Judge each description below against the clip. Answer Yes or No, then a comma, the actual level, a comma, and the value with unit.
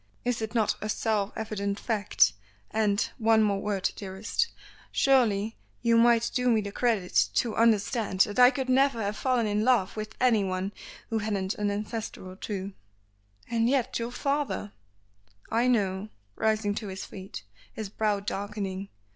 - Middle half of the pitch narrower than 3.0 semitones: Yes, narrow, 2.6 semitones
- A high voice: Yes, high, 215 Hz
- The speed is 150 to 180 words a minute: Yes, average, 160 wpm